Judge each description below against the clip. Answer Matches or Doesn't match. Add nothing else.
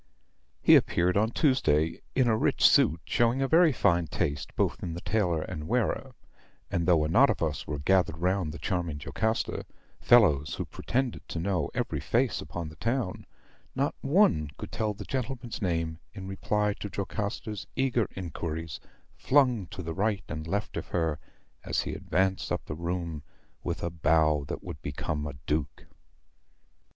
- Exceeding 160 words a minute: Matches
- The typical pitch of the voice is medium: Doesn't match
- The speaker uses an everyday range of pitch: Doesn't match